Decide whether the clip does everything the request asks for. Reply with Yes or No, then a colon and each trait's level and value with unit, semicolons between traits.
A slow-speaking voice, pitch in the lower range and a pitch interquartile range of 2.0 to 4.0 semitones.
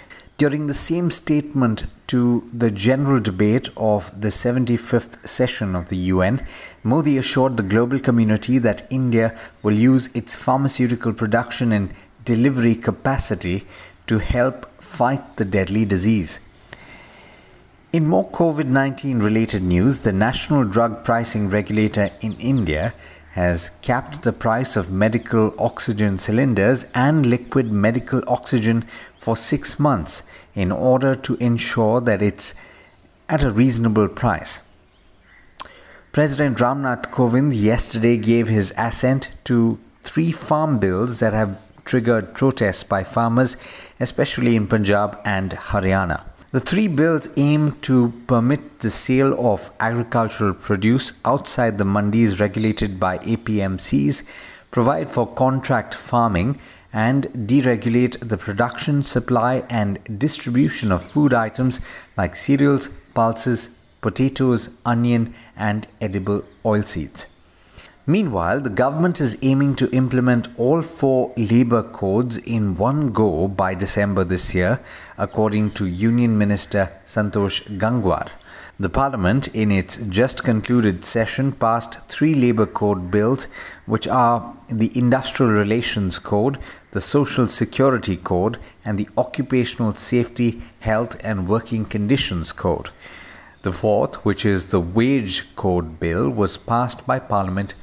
Yes: slow, 125 wpm; low, 115 Hz; average, 3.7 semitones